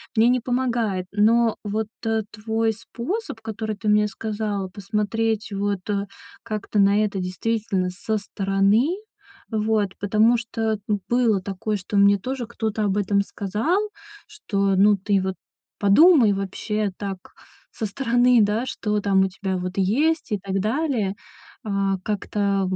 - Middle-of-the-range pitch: No, high, 210 Hz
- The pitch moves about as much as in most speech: No, narrow, 2.2 semitones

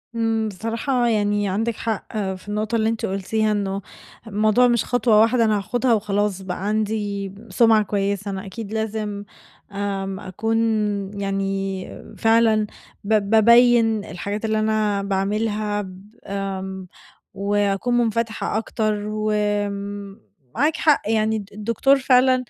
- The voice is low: No, high, 210 Hz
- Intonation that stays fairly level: Yes, narrow, 2.0 semitones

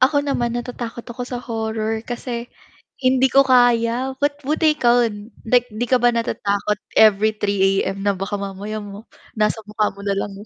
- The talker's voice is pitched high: Yes, high, 230 Hz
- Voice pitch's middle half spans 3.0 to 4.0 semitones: Yes, average, 3.3 semitones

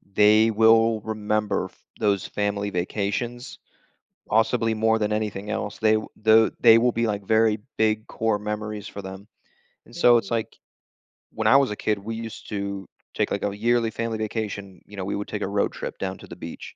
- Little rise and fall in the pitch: Yes, narrow, 1.7 semitones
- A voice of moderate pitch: No, low, 110 Hz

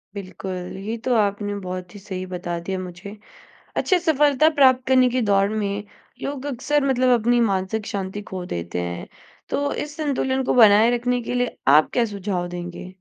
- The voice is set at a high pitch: Yes, high, 205 Hz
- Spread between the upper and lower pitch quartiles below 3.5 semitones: No, wide, 5.5 semitones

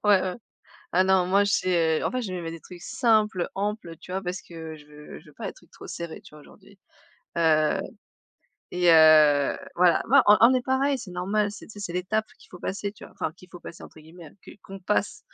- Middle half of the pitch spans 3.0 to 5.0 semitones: Yes, average, 3.8 semitones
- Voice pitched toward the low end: No, medium, 180 Hz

